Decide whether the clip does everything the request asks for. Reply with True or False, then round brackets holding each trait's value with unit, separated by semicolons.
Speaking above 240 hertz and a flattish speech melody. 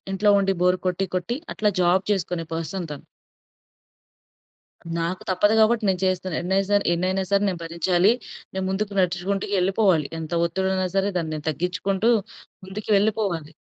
False (185 Hz; 2.2 semitones)